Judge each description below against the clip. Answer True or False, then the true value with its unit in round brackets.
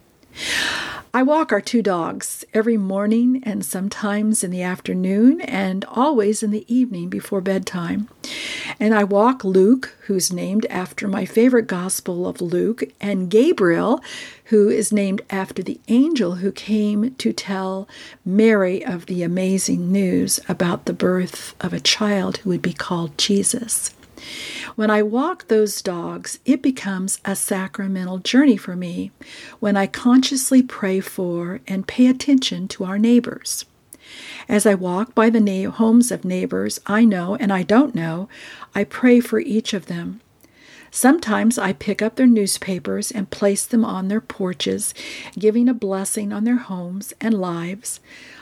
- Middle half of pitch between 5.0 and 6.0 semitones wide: False (3.4 semitones)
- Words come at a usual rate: True (150 wpm)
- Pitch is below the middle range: False (205 Hz)